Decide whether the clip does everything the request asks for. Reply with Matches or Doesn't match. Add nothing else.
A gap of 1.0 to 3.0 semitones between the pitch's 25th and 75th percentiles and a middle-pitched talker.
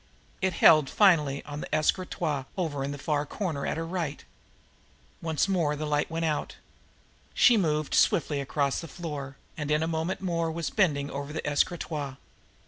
Matches